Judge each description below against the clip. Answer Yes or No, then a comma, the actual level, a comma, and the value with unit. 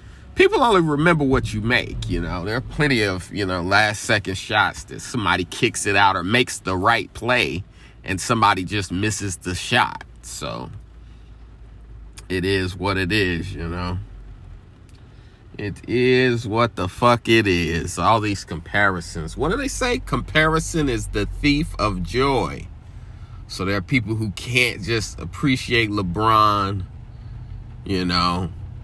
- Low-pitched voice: Yes, low, 105 Hz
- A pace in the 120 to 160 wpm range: Yes, average, 150 wpm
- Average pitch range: Yes, average, 4.1 semitones